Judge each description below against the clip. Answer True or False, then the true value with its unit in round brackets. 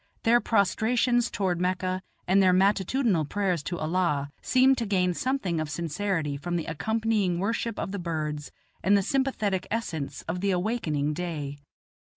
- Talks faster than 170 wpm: False (155 wpm)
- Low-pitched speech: False (185 Hz)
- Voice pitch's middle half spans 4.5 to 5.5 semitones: True (4.9 semitones)